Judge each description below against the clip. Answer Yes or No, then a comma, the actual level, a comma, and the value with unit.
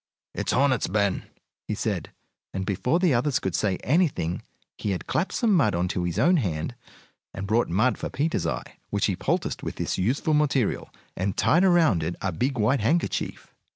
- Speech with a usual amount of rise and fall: No, wide, 8.1 semitones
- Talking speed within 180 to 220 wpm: Yes, average, 185 wpm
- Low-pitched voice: Yes, low, 120 Hz